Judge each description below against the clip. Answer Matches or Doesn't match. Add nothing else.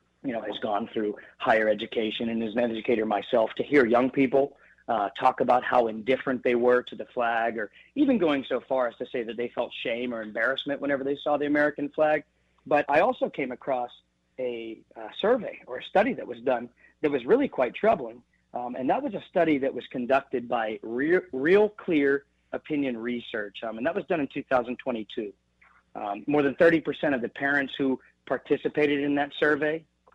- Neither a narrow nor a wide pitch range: Matches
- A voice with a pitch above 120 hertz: Matches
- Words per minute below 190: Doesn't match